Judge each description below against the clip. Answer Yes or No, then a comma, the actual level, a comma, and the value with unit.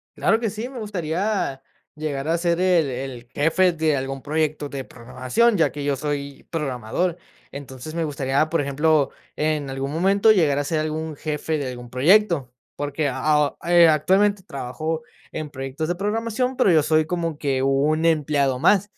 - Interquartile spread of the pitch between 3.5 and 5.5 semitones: Yes, average, 3.8 semitones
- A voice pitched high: No, medium, 155 Hz